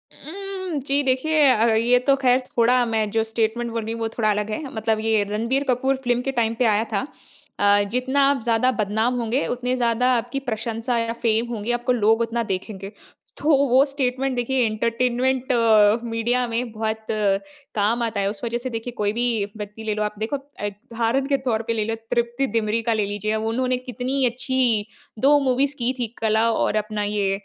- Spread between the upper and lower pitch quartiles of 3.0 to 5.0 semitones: No, narrow, 2.6 semitones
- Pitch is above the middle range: Yes, high, 235 Hz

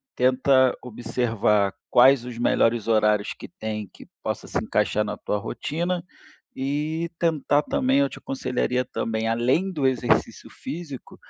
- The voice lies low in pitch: Yes, low, 125 Hz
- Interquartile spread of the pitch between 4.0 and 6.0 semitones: Yes, average, 5.3 semitones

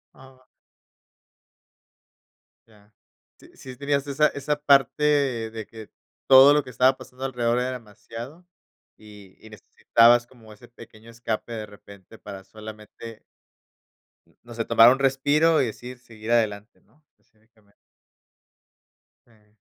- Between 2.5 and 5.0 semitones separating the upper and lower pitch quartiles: Yes, average, 3.4 semitones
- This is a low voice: Yes, low, 120 Hz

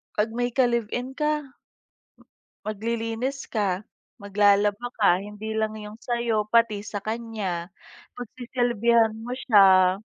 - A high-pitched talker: Yes, high, 220 Hz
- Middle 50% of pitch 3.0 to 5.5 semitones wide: No, narrow, 2.6 semitones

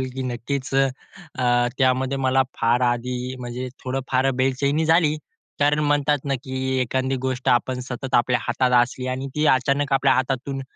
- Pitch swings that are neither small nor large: No, narrow, 1.4 semitones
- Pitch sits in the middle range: No, low, 130 Hz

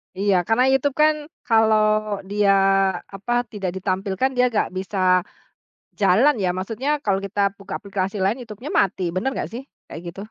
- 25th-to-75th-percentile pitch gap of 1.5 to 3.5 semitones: No, average, 3.9 semitones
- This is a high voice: Yes, high, 205 Hz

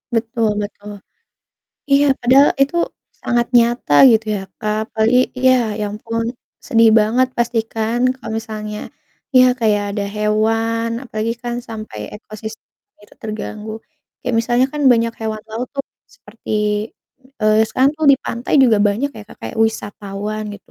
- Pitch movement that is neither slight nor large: No, narrow, 2.0 semitones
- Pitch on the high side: Yes, high, 225 Hz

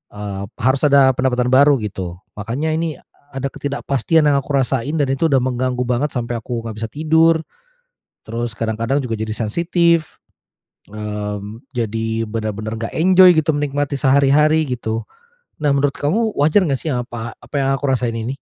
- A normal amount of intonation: Yes, average, 4.3 semitones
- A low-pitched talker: Yes, low, 130 Hz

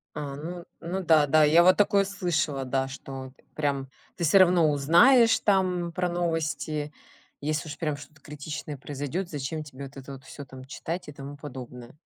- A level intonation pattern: No, average, 3.8 semitones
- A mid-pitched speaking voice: Yes, medium, 150 Hz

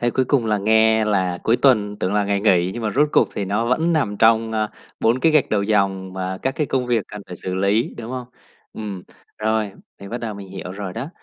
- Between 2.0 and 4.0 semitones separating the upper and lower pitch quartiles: Yes, average, 3.1 semitones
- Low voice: Yes, low, 110 Hz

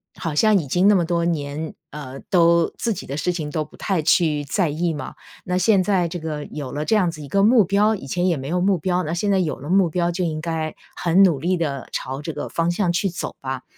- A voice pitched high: No, medium, 170 Hz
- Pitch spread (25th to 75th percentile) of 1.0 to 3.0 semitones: No, average, 3.4 semitones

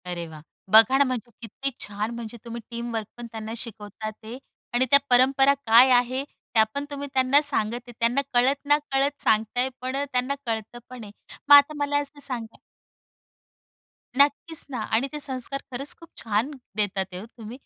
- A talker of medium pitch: No, high, 245 Hz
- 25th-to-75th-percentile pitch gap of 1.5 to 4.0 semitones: Yes, average, 3.7 semitones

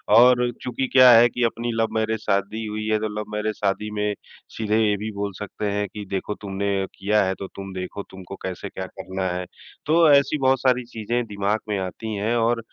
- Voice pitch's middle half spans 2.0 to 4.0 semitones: Yes, average, 2.8 semitones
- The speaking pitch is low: Yes, low, 105 Hz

